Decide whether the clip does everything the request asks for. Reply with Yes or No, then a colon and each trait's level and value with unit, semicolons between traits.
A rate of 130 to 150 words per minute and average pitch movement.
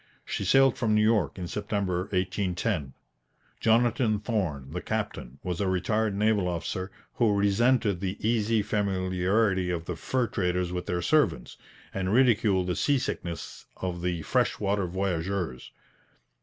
Yes: average, 140 wpm; average, 3.5 semitones